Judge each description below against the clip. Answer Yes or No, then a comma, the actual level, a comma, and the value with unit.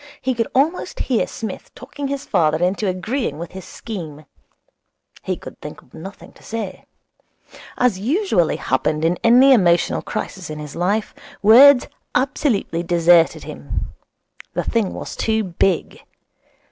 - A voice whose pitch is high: Yes, high, 200 Hz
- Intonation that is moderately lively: No, wide, 6.5 semitones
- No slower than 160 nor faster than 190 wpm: No, average, 140 wpm